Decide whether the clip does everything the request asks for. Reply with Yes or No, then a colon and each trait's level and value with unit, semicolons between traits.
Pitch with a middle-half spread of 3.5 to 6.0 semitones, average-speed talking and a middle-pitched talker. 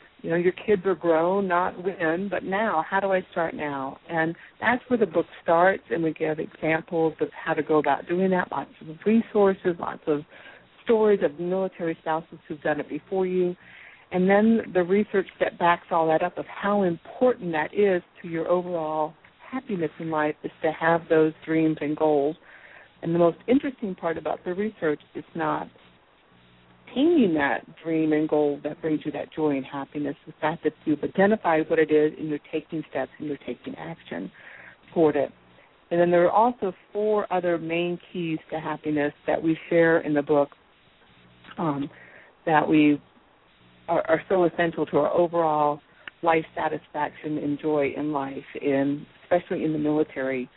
No: average, 3.1 semitones; average, 180 wpm; medium, 165 Hz